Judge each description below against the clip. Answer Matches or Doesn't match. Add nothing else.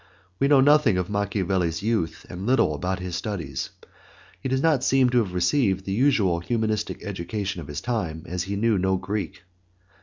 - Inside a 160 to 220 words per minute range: Matches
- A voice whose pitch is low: Matches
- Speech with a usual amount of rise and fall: Matches